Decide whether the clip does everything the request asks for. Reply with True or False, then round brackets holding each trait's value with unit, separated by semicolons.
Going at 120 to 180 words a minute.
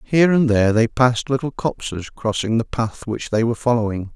False (200 wpm)